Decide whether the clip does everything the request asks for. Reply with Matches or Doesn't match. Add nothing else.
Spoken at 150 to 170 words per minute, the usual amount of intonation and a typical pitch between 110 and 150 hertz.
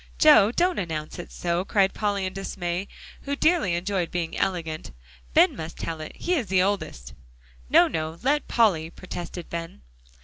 Doesn't match